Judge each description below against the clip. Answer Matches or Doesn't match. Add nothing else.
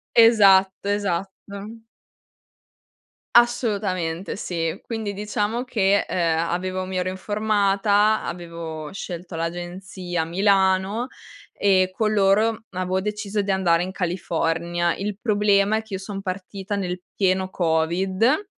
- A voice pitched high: Matches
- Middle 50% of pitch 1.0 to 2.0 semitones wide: Doesn't match